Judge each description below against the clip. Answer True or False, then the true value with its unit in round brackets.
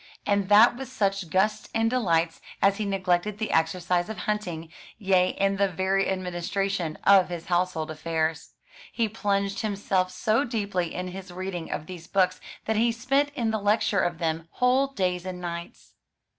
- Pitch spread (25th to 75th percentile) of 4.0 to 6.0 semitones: False (3.2 semitones)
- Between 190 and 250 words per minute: False (170 wpm)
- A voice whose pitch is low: False (190 Hz)